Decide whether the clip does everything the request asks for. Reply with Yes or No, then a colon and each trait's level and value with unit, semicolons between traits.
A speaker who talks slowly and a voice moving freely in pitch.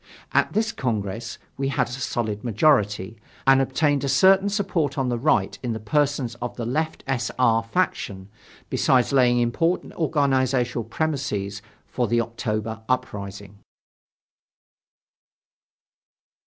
No: slow, 125 wpm; average, 4.2 semitones